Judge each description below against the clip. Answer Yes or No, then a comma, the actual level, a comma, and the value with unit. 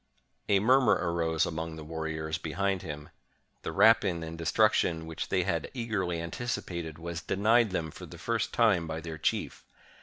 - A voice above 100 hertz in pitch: No, very low, 85 Hz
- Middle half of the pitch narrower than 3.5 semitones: No, average, 4.2 semitones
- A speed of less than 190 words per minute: Yes, average, 170 wpm